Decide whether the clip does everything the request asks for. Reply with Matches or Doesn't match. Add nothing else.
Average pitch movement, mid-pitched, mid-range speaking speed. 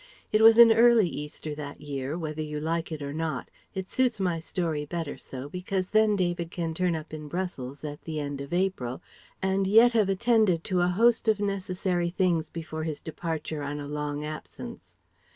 Matches